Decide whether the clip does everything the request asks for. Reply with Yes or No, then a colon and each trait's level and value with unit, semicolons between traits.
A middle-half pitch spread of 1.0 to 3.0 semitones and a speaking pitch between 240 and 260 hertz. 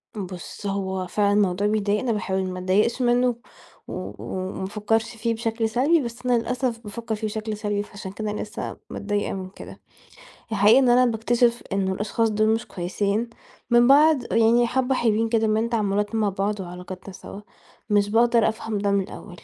No: narrow, 2.6 semitones; high, 215 Hz